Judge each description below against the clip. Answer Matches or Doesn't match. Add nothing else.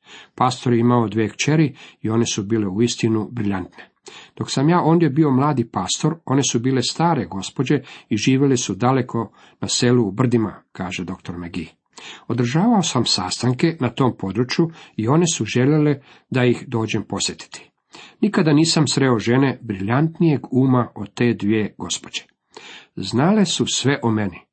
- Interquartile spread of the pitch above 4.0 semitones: Matches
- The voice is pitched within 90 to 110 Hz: Doesn't match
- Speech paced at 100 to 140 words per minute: Doesn't match